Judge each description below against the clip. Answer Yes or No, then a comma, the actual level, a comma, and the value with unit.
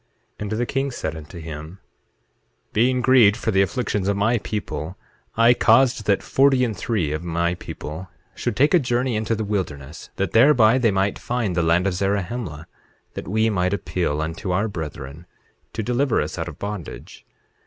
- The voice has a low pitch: Yes, low, 100 Hz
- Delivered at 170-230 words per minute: Yes, average, 180 wpm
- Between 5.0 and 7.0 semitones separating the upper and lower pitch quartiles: Yes, wide, 5.5 semitones